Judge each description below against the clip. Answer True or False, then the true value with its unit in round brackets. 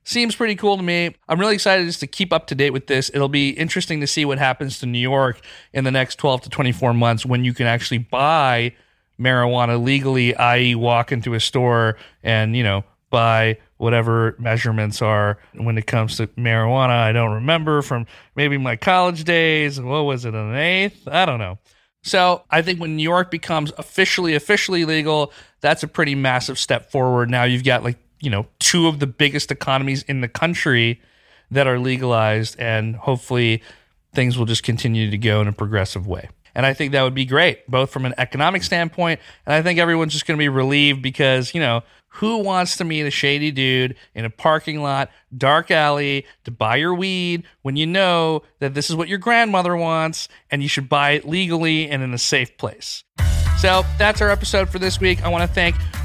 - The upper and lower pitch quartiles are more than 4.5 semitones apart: True (5.0 semitones)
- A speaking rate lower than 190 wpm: False (205 wpm)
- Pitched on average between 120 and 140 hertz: True (135 Hz)